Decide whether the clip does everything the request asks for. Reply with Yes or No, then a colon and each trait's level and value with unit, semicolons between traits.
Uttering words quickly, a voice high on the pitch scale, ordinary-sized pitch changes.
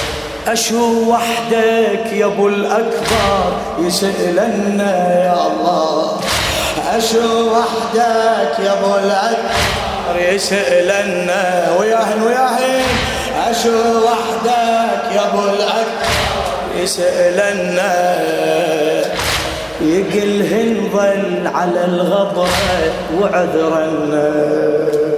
No: slow, 65 wpm; high, 205 Hz; average, 4.2 semitones